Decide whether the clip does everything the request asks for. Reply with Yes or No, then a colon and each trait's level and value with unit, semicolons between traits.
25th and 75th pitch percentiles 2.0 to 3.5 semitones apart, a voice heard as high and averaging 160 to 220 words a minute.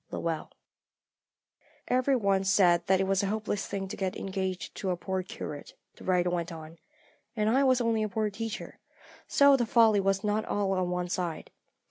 Yes: average, 3.1 semitones; high, 195 Hz; average, 185 wpm